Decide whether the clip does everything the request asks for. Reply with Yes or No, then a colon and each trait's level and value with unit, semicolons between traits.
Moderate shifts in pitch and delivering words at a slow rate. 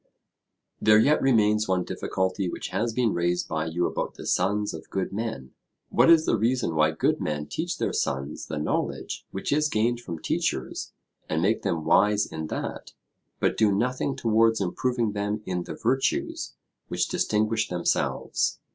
No: average, 4.6 semitones; average, 165 wpm